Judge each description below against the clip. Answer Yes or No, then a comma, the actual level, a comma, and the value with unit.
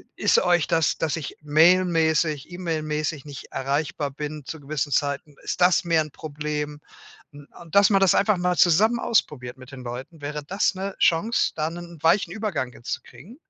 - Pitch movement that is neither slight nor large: Yes, average, 3.5 semitones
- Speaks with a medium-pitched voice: Yes, medium, 155 Hz